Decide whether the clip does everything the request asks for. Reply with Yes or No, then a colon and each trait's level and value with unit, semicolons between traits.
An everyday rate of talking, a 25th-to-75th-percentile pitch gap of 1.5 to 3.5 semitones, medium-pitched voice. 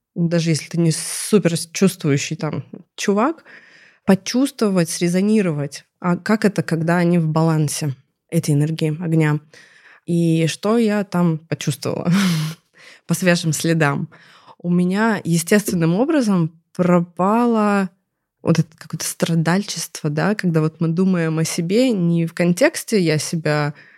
Yes: average, 125 wpm; average, 2.9 semitones; medium, 170 Hz